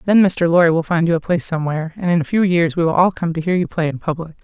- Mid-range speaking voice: Yes, medium, 170 Hz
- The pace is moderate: No, fast, 325 wpm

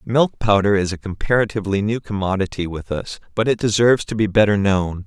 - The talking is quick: No, average, 190 wpm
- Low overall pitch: Yes, low, 105 Hz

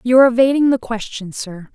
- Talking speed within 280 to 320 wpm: No, fast, 205 wpm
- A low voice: No, high, 240 Hz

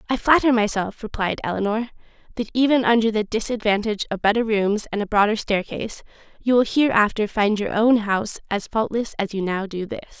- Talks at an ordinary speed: Yes, average, 180 wpm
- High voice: Yes, high, 220 Hz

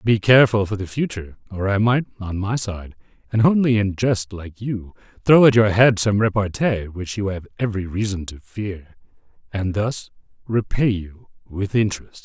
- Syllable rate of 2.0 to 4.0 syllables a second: No, 5.0 syllables/s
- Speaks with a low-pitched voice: Yes, low, 105 Hz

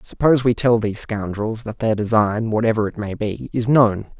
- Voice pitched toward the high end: No, low, 110 Hz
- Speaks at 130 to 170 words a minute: No, average, 200 wpm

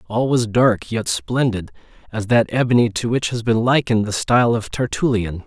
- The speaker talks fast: No, average, 175 wpm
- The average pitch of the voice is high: No, low, 115 Hz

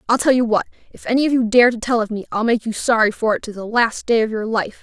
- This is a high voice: Yes, high, 230 Hz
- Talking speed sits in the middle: No, fast, 325 wpm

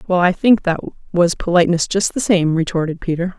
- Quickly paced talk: No, average, 195 wpm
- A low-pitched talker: No, medium, 175 Hz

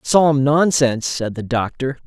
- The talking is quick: No, average, 145 wpm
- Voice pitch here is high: No, low, 135 Hz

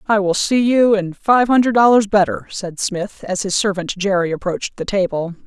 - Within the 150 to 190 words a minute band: No, average, 200 wpm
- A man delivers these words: No, female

